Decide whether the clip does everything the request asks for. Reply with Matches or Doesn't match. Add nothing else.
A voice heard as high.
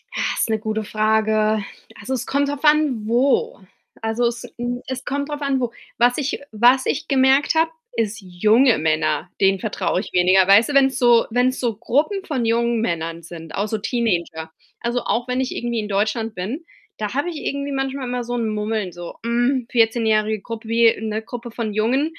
Matches